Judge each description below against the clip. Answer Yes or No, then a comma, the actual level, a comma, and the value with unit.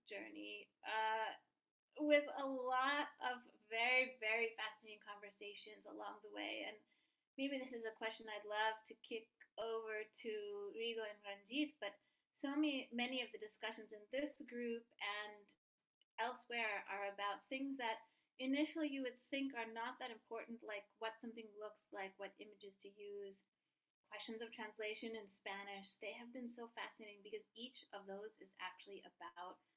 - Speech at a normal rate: Yes, average, 155 wpm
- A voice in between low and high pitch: No, high, 225 Hz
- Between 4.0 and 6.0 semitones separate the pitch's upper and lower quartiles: No, average, 3.3 semitones